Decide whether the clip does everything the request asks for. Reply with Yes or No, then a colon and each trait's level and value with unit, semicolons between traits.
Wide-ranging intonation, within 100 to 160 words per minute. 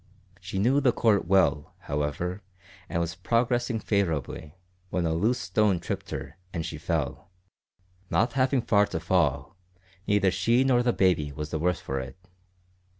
Yes: wide, 6.1 semitones; average, 155 wpm